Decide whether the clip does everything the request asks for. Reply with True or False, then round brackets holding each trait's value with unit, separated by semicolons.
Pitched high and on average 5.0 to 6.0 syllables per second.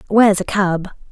True (195 Hz; 5.1 syllables/s)